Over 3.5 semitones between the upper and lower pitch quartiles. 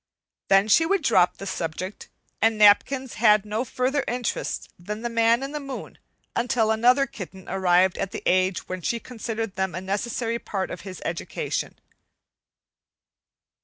Yes: average, 4.1 semitones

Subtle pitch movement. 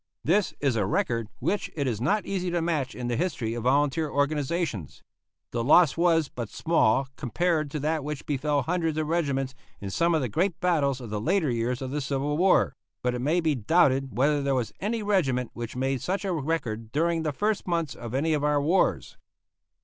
No: average, 4.9 semitones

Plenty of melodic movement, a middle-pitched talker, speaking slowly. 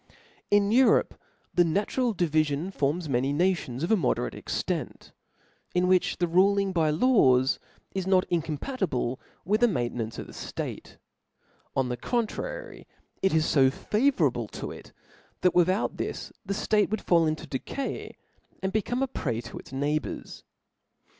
No: wide, 6.1 semitones; medium, 180 Hz; average, 160 wpm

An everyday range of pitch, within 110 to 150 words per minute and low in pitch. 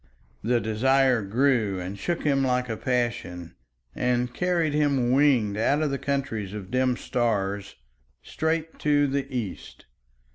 Yes: average, 4.6 semitones; average, 140 wpm; low, 125 Hz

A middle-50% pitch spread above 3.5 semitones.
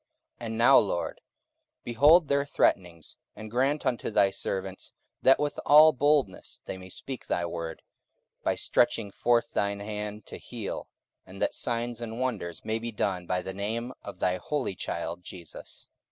Yes: average, 4.8 semitones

